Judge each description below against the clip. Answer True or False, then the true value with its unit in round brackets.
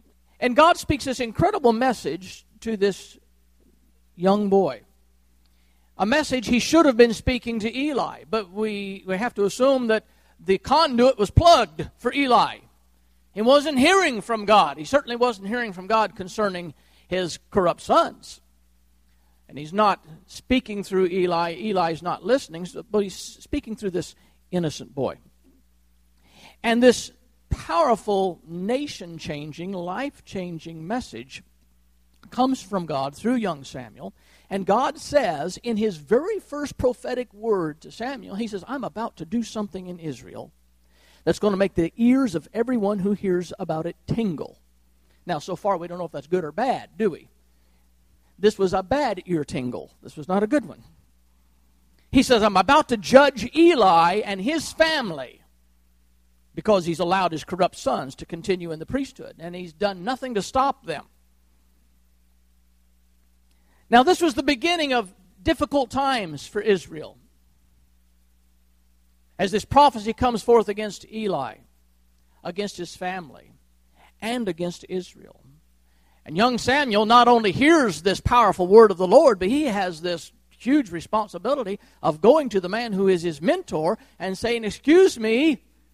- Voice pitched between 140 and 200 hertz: True (190 Hz)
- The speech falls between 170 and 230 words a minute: False (150 wpm)